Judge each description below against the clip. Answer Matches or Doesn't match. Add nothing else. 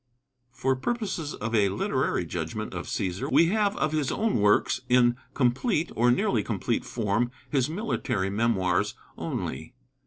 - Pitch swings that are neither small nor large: Doesn't match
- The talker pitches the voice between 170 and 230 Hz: Doesn't match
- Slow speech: Doesn't match